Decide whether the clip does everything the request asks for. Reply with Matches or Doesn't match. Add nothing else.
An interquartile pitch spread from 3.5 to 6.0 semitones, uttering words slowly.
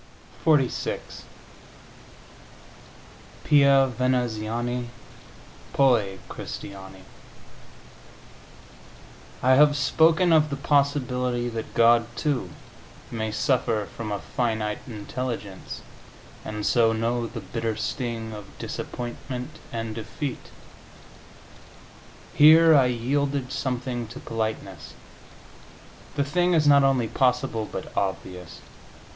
Matches